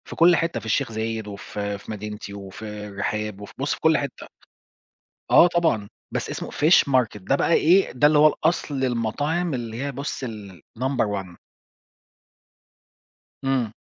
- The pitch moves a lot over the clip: Yes, wide, 5.9 semitones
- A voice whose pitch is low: Yes, low, 120 Hz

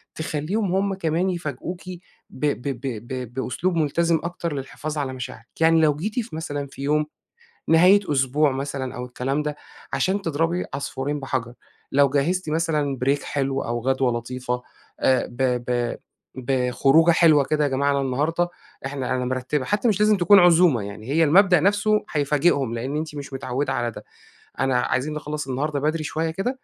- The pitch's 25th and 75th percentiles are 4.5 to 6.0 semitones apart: No, average, 4.0 semitones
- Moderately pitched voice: Yes, medium, 145 Hz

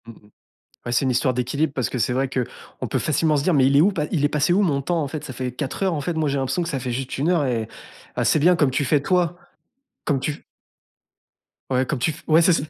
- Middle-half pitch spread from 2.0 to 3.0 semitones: No, average, 3.7 semitones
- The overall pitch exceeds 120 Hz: Yes, medium, 140 Hz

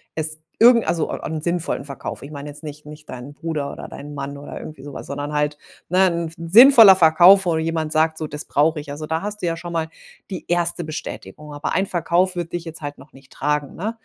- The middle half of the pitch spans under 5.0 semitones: Yes, average, 2.8 semitones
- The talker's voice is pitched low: No, medium, 160 Hz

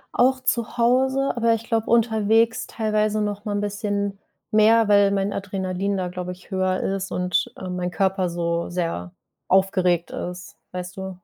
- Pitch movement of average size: Yes, average, 3.3 semitones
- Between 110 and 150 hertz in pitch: No, high, 200 Hz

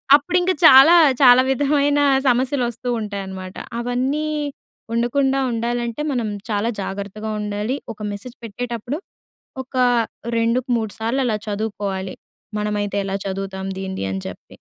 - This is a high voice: Yes, high, 230 Hz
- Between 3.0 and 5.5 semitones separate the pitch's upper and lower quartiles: Yes, average, 4.2 semitones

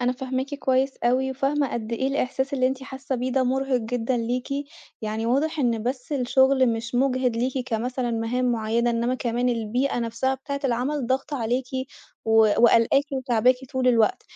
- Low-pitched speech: No, very high, 255 Hz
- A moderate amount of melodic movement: No, narrow, 2.1 semitones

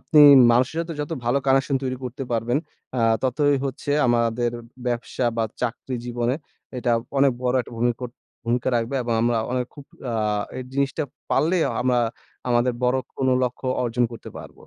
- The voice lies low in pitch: Yes, low, 125 Hz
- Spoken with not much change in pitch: Yes, narrow, 2.0 semitones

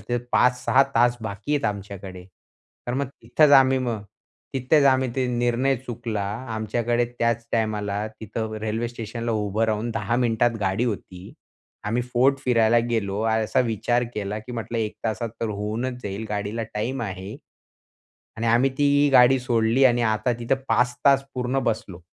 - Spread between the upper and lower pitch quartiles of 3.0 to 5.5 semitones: No, narrow, 2.5 semitones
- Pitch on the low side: Yes, low, 115 Hz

